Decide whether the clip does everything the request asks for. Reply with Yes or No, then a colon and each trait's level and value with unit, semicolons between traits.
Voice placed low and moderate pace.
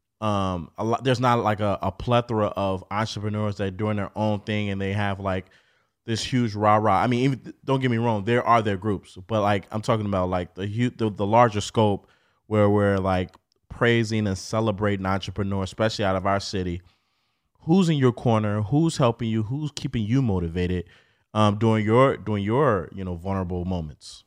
Yes: low, 105 Hz; average, 195 wpm